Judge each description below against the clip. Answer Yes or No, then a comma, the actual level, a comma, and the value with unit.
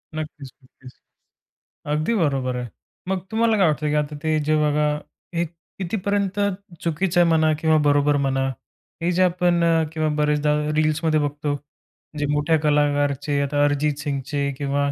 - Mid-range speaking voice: Yes, medium, 150 Hz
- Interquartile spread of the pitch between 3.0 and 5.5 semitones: No, narrow, 2.4 semitones